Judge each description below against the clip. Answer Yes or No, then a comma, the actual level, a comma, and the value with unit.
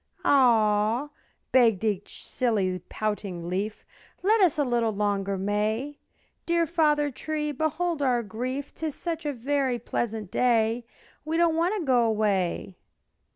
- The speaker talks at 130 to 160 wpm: Yes, average, 140 wpm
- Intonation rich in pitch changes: Yes, wide, 6.0 semitones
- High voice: Yes, high, 240 Hz